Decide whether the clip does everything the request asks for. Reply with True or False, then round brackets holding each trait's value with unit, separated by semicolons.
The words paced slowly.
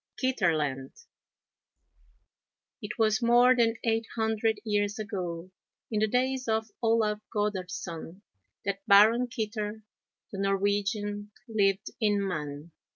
True (105 wpm)